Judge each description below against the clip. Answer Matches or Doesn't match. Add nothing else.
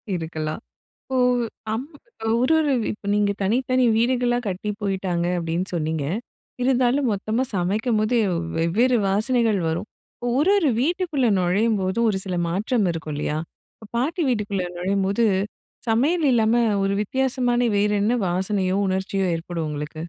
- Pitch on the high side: Matches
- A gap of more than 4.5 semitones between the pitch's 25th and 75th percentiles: Matches